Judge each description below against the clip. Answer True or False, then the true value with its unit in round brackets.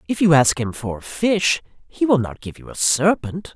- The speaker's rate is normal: False (235 wpm)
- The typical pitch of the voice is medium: True (155 Hz)